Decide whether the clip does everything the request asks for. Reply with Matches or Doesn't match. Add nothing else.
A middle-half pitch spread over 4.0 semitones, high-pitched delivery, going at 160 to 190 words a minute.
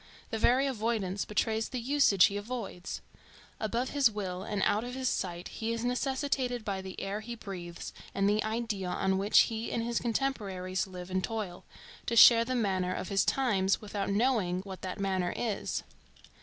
Doesn't match